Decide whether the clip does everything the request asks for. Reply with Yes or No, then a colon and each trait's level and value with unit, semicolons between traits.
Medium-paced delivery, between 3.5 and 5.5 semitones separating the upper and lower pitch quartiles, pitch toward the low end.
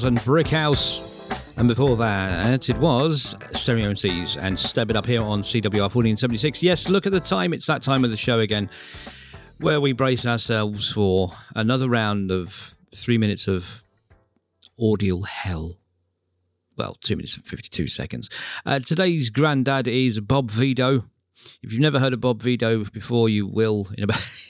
Yes: average, 175 wpm; average, 4.4 semitones; low, 115 Hz